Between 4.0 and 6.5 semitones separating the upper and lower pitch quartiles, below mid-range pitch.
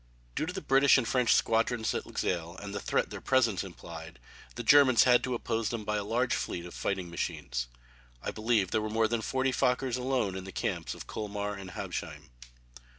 Yes: average, 4.5 semitones; low, 110 Hz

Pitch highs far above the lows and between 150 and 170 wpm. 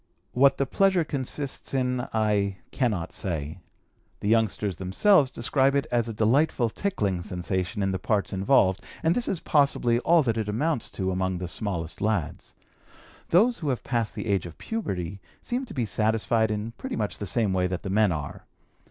No: wide, 6.2 semitones; average, 180 wpm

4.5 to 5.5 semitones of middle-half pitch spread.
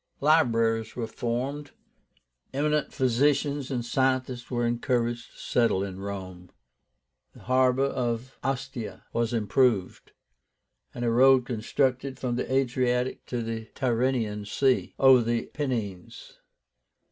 No: narrow, 2.5 semitones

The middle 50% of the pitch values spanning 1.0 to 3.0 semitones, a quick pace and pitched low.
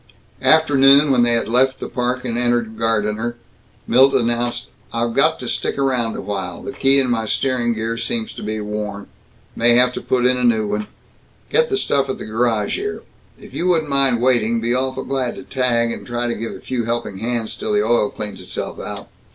Yes: average, 2.7 semitones; fast, 215 wpm; low, 120 Hz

